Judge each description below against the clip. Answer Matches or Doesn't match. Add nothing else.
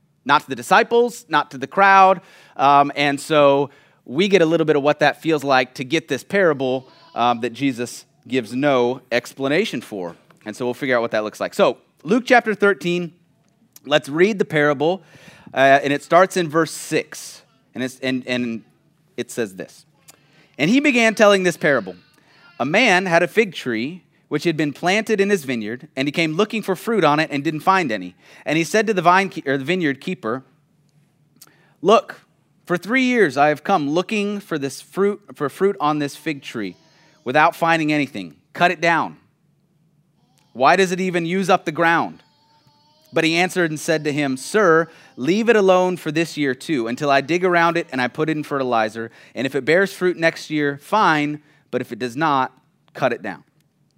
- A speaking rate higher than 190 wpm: Matches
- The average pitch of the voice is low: Doesn't match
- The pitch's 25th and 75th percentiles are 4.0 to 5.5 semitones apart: Matches